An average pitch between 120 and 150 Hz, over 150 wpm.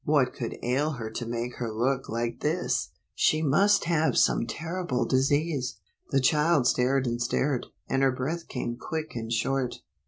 Yes: low, 135 Hz; average, 165 wpm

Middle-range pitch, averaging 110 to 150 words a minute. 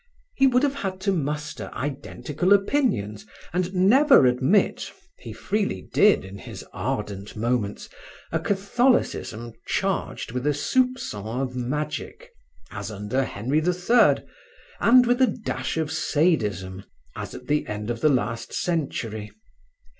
Yes: medium, 150 Hz; slow, 135 wpm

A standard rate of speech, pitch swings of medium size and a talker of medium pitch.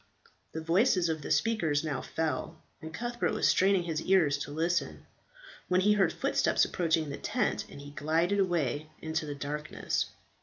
Yes: average, 165 wpm; average, 3.4 semitones; medium, 160 Hz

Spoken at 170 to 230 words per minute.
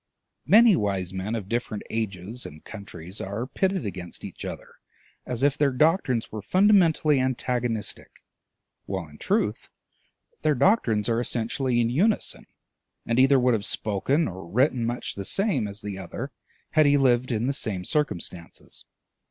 No: average, 150 wpm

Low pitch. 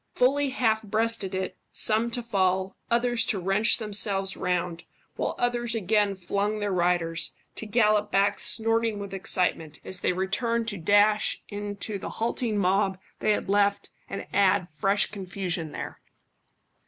No: high, 205 Hz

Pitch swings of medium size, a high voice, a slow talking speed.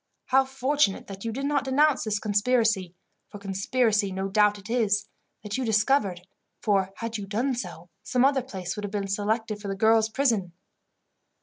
No: average, 4.2 semitones; high, 215 Hz; average, 180 wpm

